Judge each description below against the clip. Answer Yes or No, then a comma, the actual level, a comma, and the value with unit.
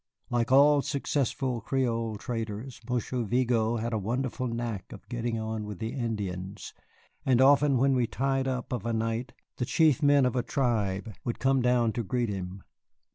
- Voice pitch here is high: No, low, 120 Hz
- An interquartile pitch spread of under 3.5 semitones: Yes, average, 2.8 semitones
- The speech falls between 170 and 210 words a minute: Yes, average, 175 wpm